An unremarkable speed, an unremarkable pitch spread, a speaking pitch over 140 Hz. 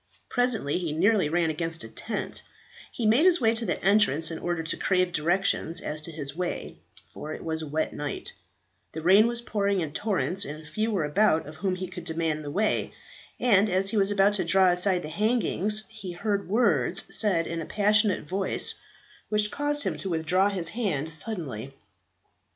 Yes: average, 190 wpm; average, 4.7 semitones; medium, 185 Hz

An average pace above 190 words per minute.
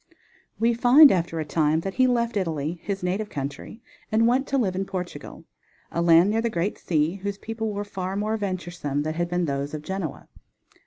Yes: average, 200 wpm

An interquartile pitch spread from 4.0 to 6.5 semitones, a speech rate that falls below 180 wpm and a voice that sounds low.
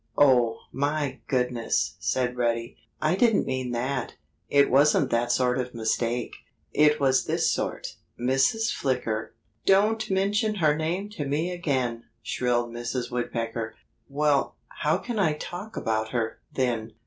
Yes: average, 4.4 semitones; slow, 135 wpm; low, 130 Hz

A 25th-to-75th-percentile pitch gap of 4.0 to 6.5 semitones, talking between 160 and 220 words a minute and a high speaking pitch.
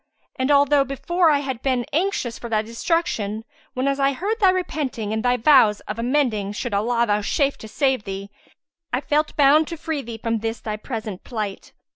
Yes: average, 4.9 semitones; average, 185 wpm; very high, 250 Hz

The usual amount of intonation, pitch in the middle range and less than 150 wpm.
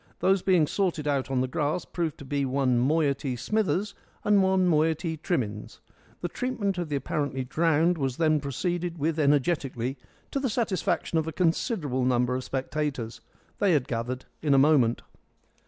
No: average, 4.8 semitones; medium, 150 Hz; average, 170 wpm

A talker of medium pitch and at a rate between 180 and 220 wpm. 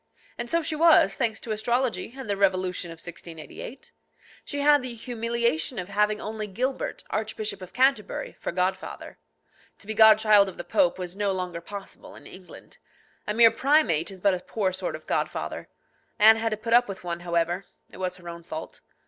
No: high, 210 Hz; average, 190 wpm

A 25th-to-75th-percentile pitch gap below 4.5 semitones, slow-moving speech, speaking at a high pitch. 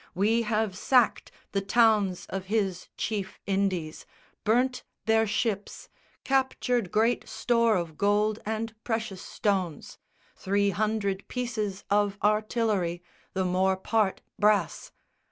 Yes: narrow, 2.6 semitones; slow, 115 wpm; high, 210 Hz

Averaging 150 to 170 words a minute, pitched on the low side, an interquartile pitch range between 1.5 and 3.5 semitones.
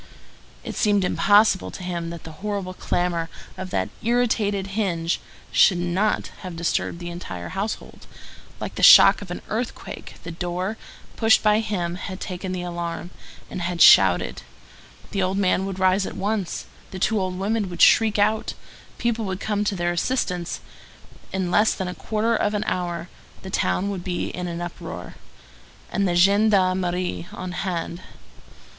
No: average, 165 wpm; medium, 185 Hz; average, 2.8 semitones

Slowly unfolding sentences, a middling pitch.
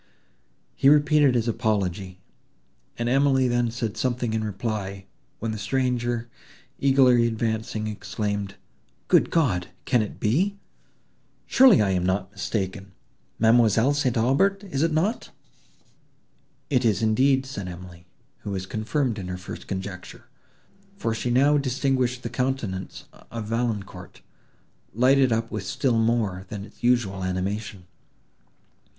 No: slow, 120 wpm; low, 115 Hz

